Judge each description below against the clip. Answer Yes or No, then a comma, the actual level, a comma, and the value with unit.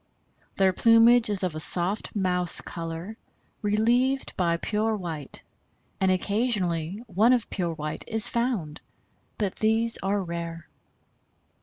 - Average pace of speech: No, slow, 125 wpm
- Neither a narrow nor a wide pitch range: Yes, average, 4.7 semitones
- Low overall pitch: No, high, 195 Hz